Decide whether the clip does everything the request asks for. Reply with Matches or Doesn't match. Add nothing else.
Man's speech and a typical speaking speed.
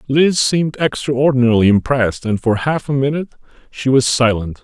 Matches